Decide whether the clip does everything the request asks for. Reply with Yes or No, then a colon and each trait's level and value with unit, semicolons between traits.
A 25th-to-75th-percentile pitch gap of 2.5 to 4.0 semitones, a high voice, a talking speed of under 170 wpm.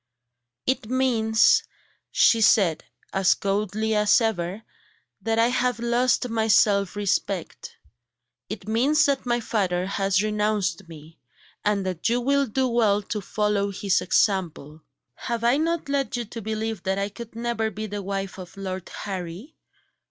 Yes: average, 3.3 semitones; high, 215 Hz; average, 150 wpm